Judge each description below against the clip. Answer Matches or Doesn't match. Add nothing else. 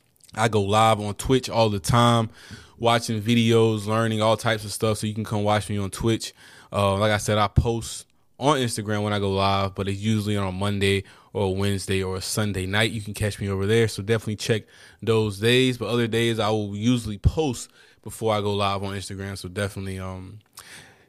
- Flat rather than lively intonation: Matches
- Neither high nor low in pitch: Doesn't match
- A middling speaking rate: Doesn't match